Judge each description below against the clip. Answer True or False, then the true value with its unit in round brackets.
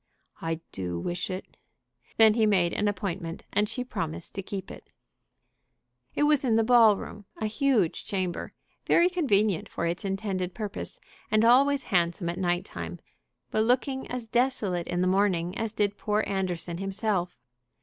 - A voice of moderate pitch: False (200 Hz)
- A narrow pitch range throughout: False (4.1 semitones)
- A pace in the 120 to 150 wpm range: False (160 wpm)